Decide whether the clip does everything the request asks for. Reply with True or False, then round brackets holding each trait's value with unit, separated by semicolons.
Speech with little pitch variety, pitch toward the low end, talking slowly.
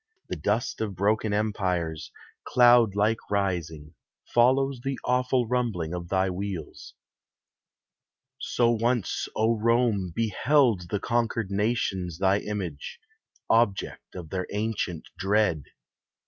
False (4.2 semitones; 105 Hz; 110 wpm)